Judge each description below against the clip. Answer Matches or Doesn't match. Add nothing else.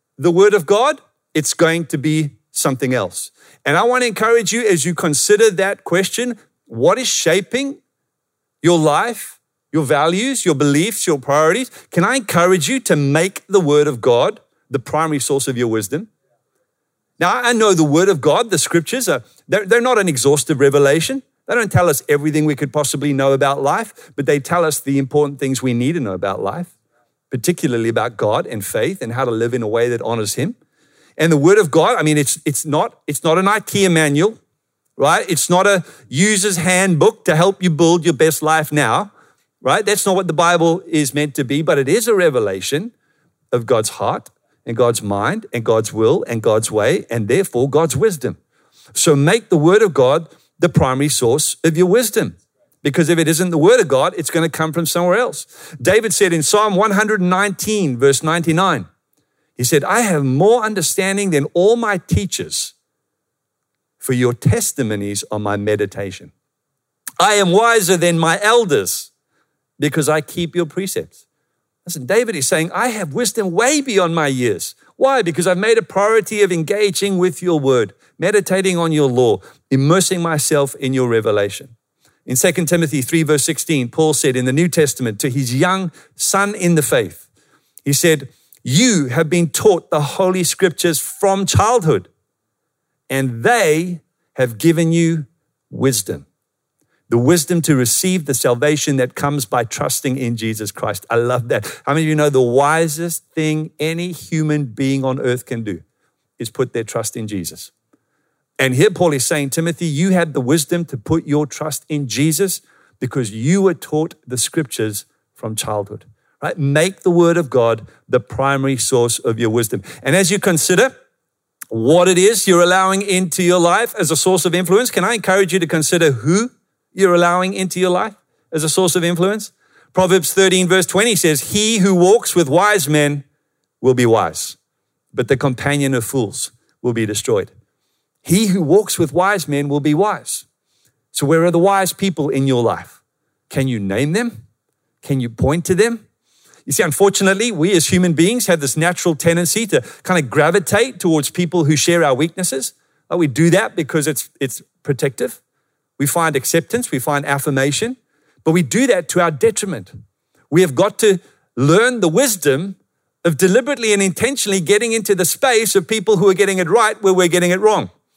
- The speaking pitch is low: Doesn't match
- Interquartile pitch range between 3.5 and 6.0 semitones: Matches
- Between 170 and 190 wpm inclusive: Matches